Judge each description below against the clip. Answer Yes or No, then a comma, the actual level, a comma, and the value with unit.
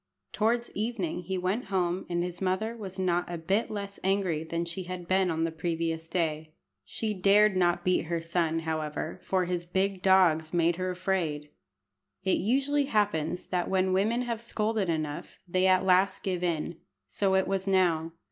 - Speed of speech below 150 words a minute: No, average, 175 wpm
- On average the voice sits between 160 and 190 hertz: Yes, medium, 185 Hz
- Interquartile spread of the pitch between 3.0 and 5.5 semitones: No, narrow, 2.6 semitones